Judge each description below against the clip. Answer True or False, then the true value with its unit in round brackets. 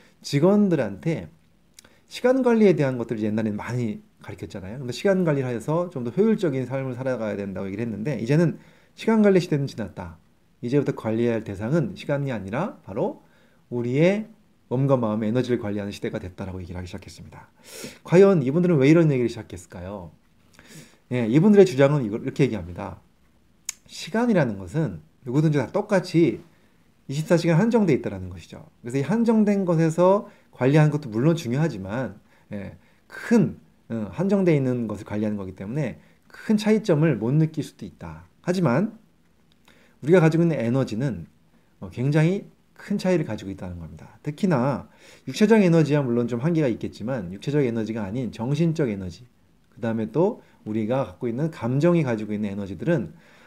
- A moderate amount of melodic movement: False (7.9 semitones)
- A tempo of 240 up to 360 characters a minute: False (375 characters per minute)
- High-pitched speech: False (135 Hz)